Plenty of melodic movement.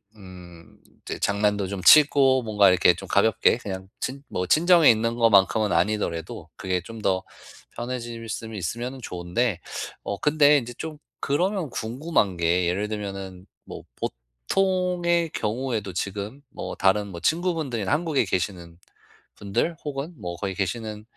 Yes: wide, 6.4 semitones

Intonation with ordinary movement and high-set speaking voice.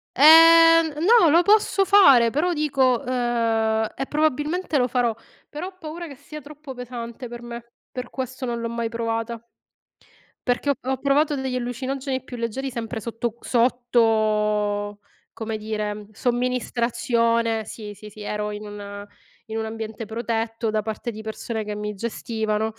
Yes: average, 3.5 semitones; high, 235 Hz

